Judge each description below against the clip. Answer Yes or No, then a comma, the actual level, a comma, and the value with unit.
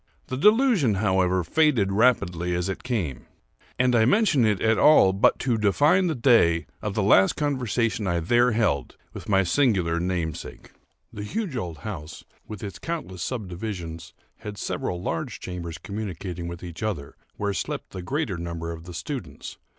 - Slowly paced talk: No, average, 165 wpm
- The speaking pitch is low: Yes, low, 100 Hz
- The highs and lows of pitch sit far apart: Yes, wide, 5.9 semitones